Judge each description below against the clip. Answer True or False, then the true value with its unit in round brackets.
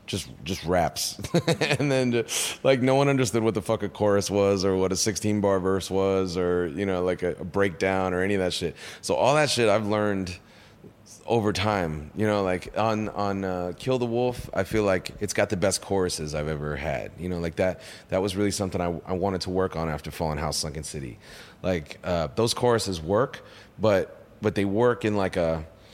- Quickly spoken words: True (215 wpm)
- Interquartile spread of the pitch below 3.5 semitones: True (3.1 semitones)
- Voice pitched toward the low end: True (95 Hz)